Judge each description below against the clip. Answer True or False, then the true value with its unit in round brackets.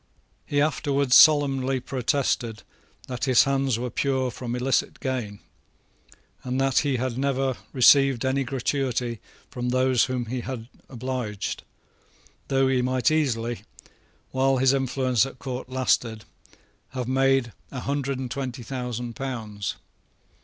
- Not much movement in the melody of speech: True (1.7 semitones)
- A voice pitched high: False (130 Hz)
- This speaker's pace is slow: True (130 wpm)